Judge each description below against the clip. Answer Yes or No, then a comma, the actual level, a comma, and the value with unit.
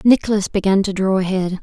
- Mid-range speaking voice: No, high, 195 Hz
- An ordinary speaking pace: Yes, average, 185 wpm